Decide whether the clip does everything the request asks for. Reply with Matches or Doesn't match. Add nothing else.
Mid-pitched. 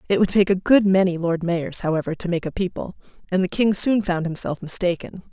Matches